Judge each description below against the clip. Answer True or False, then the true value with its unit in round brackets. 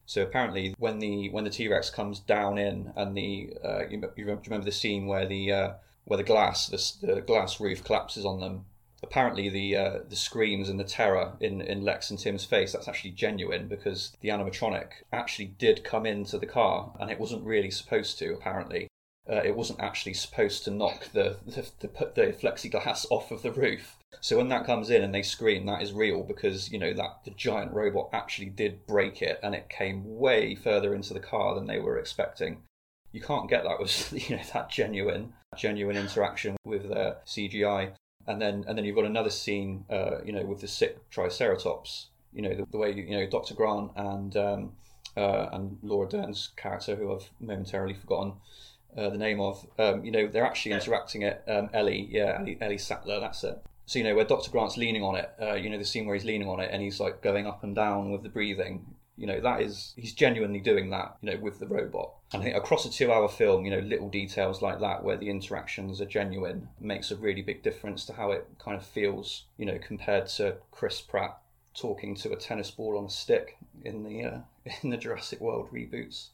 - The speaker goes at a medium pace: False (215 wpm)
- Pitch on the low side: True (105 Hz)